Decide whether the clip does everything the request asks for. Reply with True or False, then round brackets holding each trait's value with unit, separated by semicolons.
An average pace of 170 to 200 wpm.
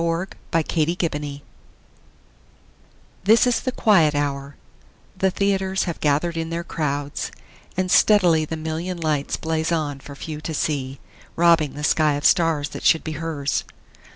False (150 wpm)